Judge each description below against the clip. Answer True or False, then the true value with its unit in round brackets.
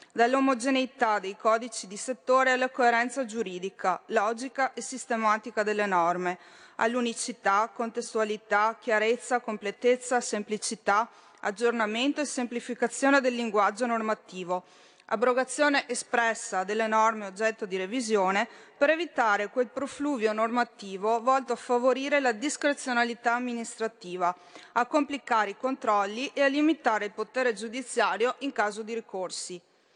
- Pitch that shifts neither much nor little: True (3.3 semitones)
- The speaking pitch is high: True (235 Hz)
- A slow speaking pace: True (110 wpm)